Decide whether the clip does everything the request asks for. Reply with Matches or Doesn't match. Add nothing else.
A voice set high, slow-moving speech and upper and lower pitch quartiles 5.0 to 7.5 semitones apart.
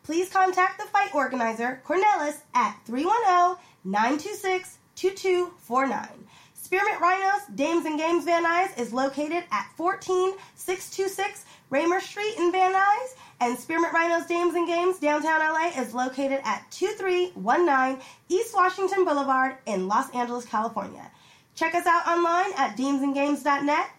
Matches